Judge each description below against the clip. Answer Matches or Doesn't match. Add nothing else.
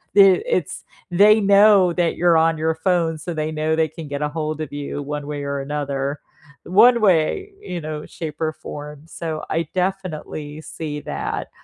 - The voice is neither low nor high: Matches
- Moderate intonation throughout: Matches